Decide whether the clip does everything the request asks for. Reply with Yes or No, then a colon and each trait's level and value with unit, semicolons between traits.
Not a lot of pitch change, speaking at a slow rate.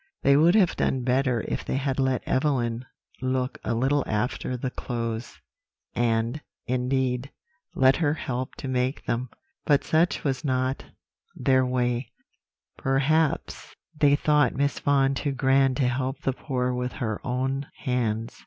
No: narrow, 1.9 semitones; average, 145 wpm